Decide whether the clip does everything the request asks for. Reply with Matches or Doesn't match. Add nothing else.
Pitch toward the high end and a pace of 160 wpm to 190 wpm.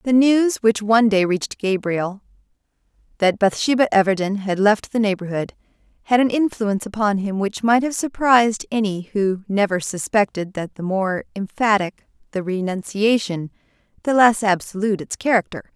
Doesn't match